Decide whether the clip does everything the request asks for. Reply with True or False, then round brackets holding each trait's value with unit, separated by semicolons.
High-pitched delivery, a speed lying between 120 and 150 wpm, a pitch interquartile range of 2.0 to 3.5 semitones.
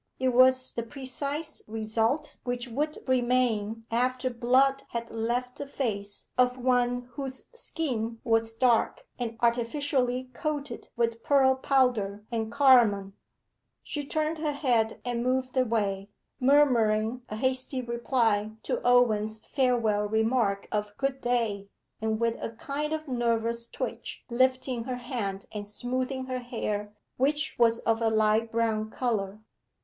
True (240 Hz; 135 wpm; 2.7 semitones)